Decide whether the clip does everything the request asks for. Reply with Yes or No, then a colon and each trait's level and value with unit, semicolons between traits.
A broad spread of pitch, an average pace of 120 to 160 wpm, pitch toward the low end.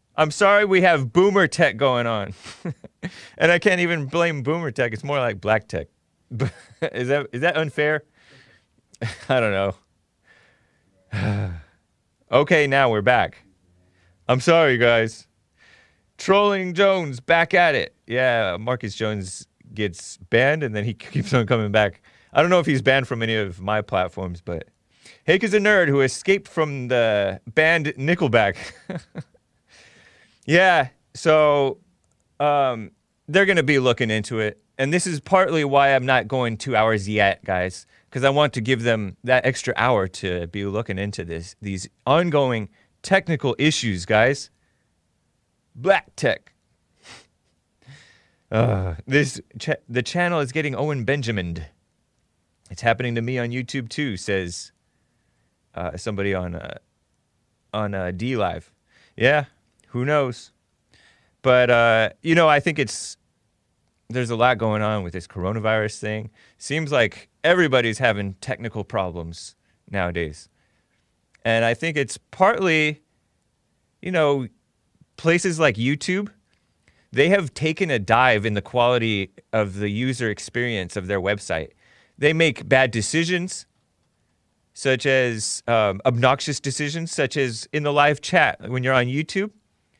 Yes: wide, 6.0 semitones; average, 140 wpm; low, 120 Hz